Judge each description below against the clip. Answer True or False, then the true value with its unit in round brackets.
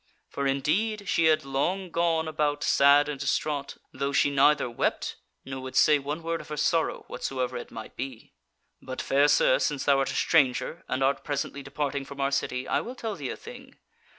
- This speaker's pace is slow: False (200 wpm)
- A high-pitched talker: False (145 Hz)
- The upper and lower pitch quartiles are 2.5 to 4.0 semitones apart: True (2.9 semitones)